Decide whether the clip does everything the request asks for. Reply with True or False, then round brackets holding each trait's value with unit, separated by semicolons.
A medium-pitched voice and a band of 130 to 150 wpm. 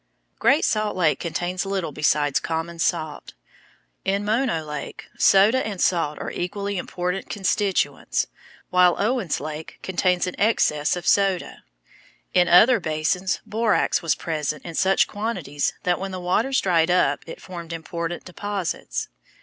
True (180 Hz; 140 wpm)